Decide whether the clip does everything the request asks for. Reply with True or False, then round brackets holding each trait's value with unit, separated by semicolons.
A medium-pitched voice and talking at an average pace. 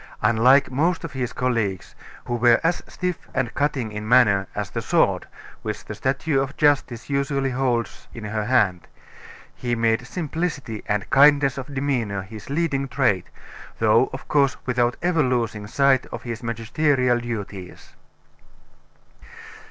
False (125 Hz; 145 wpm)